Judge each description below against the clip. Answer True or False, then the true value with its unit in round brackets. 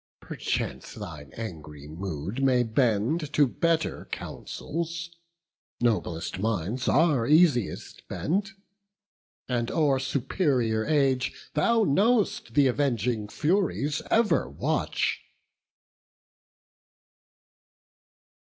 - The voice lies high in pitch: False (130 Hz)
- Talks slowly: True (80 wpm)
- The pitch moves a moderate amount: False (6.1 semitones)